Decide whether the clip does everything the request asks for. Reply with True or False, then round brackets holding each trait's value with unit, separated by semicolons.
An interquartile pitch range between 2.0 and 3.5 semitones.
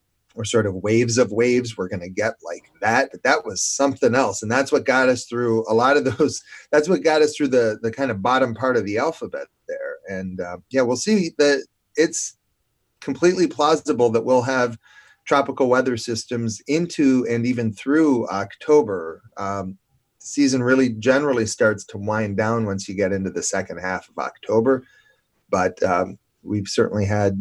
False (4.5 semitones)